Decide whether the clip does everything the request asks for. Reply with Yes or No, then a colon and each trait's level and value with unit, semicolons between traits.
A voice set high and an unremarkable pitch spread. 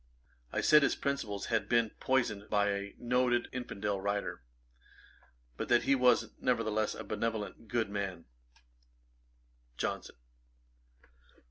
No: low, 110 Hz; average, 3.2 semitones